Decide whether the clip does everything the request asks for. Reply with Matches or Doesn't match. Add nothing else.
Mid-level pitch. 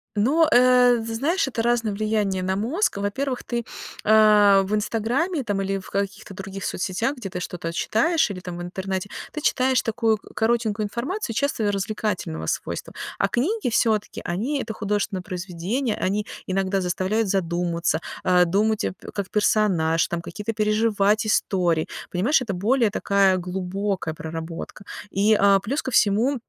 Doesn't match